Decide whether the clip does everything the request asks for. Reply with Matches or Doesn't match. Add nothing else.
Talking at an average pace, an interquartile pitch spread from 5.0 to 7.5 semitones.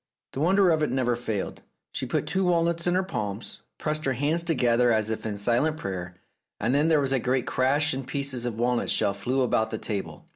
Doesn't match